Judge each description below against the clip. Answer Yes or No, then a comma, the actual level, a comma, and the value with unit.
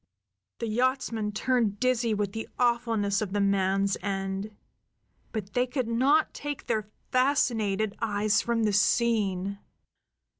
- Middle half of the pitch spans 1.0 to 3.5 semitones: Yes, average, 3.1 semitones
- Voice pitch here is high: Yes, high, 220 Hz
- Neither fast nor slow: No, slow, 125 wpm